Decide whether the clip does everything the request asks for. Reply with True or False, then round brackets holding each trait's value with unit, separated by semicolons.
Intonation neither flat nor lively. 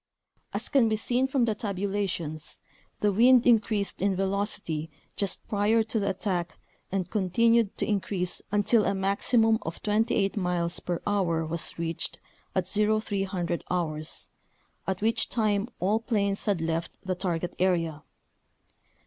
True (3.4 semitones)